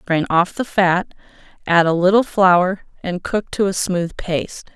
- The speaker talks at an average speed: Yes, average, 175 wpm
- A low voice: No, medium, 185 Hz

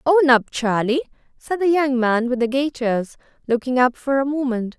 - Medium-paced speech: Yes, average, 190 wpm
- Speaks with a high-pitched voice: Yes, very high, 260 Hz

